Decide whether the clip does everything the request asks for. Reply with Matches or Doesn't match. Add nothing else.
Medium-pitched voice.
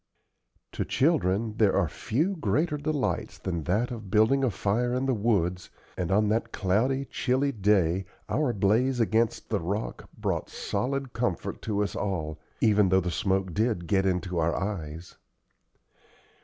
Doesn't match